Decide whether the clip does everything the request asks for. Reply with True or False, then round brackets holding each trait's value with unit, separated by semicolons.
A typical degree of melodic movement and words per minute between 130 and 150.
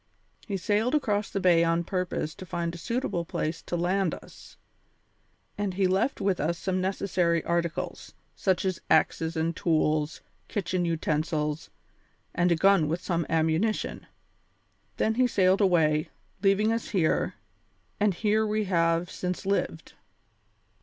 True (3.0 semitones; 140 wpm)